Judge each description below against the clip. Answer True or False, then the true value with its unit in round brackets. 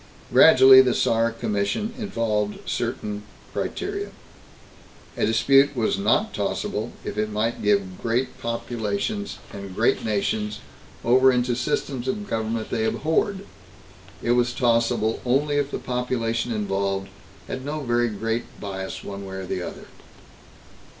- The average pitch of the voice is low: True (115 Hz)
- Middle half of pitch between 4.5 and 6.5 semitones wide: False (3.7 semitones)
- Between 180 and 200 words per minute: False (135 wpm)